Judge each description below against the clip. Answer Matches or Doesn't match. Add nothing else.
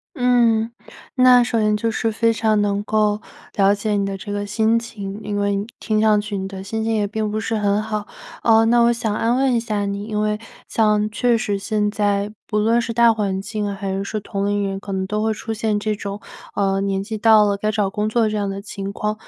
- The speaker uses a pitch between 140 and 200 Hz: Doesn't match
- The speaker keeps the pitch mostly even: Matches